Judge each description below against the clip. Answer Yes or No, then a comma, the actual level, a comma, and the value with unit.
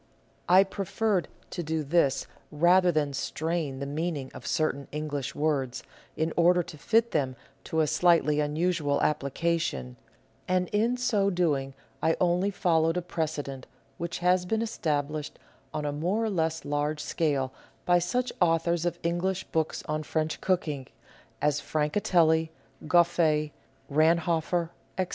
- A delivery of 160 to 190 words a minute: No, average, 140 wpm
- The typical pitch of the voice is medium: Yes, medium, 160 Hz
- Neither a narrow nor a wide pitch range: Yes, average, 3.0 semitones